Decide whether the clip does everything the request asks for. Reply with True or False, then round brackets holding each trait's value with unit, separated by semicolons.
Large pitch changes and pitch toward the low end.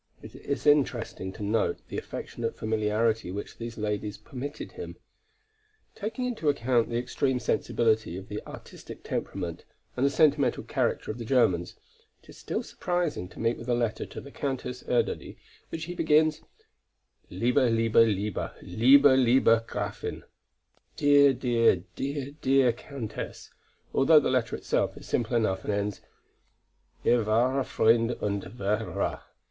False (4.0 semitones; 120 Hz)